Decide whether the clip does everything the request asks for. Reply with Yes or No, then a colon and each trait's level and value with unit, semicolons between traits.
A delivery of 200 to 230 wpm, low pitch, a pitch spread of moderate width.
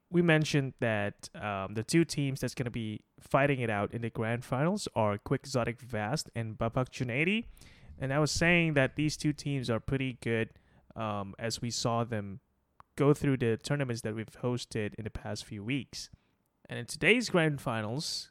No: average, 190 wpm; low, 125 Hz; average, 4.5 semitones